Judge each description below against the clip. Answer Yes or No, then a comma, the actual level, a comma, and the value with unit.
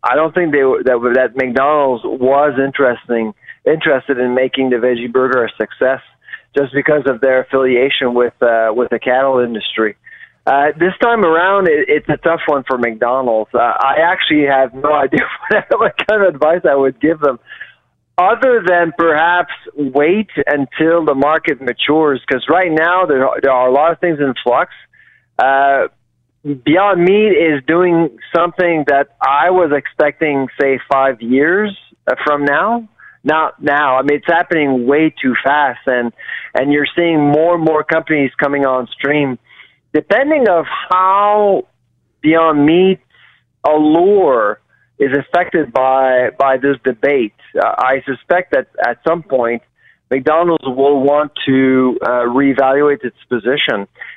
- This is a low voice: No, medium, 145 Hz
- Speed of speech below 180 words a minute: Yes, average, 155 wpm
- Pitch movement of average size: Yes, average, 4.0 semitones